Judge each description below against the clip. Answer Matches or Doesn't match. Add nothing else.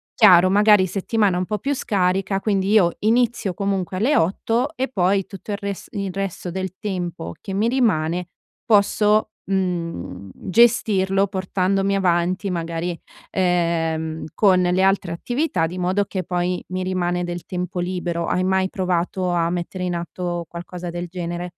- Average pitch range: Doesn't match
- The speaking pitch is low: Doesn't match